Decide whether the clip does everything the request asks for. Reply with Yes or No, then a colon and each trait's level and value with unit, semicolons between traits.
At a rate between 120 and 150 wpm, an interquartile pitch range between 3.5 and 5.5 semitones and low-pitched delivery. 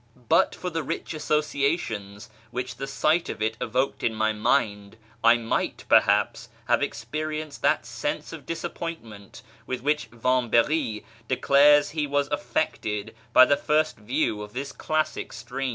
Yes: average, 145 wpm; average, 5.2 semitones; low, 130 Hz